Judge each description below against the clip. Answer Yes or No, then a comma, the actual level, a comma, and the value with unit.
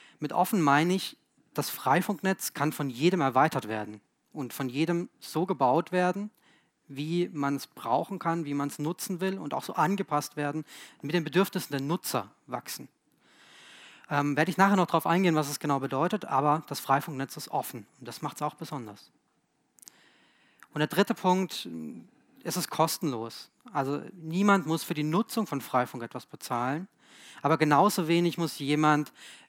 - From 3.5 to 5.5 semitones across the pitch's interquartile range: Yes, average, 4.4 semitones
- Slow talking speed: No, average, 170 wpm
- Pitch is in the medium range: Yes, medium, 160 Hz